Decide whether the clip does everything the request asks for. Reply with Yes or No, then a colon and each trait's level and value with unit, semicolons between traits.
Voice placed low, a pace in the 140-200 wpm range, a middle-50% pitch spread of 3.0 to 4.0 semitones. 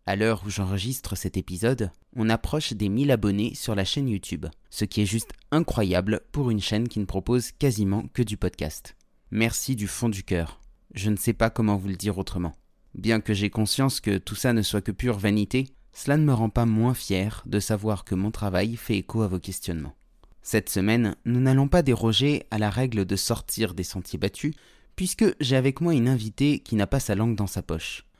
No: low, 110 Hz; average, 215 wpm; average, 3.7 semitones